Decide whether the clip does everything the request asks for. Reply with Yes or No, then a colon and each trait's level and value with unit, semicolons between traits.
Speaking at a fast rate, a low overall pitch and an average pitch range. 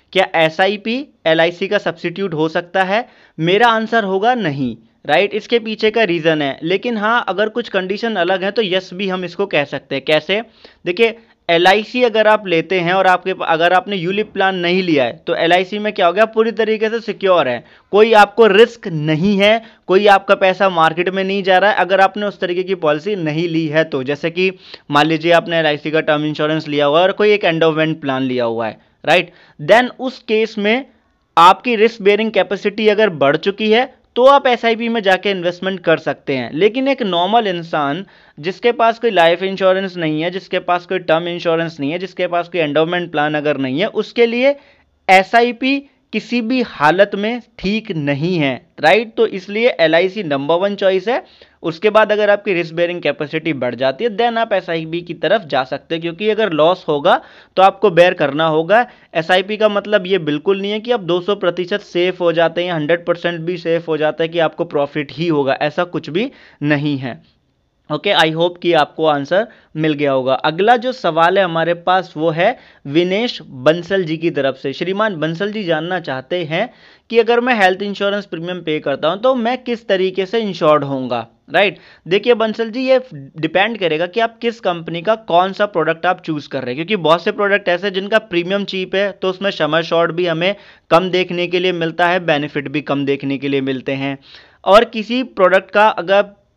No: fast, 210 wpm; medium, 185 Hz; average, 4.7 semitones